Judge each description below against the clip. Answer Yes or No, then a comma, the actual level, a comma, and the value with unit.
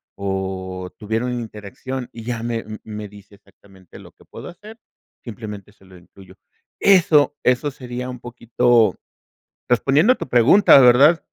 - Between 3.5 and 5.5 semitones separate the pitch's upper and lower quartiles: Yes, average, 4.0 semitones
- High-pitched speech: No, low, 115 Hz